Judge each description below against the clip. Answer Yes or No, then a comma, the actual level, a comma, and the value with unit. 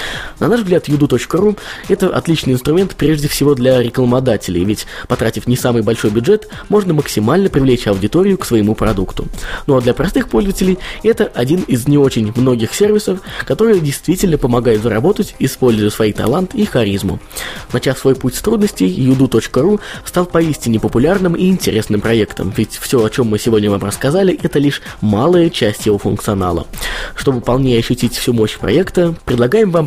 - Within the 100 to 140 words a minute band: No, fast, 160 wpm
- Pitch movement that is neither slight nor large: No, wide, 7.5 semitones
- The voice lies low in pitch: Yes, low, 130 Hz